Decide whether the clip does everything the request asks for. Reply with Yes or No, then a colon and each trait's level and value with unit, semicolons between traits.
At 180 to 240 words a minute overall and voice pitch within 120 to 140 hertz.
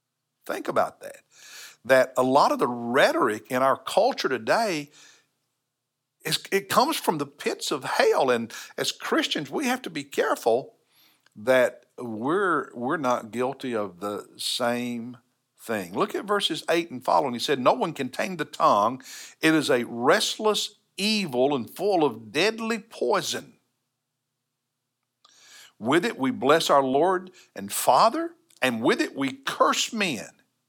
No: average, 150 wpm; low, 135 Hz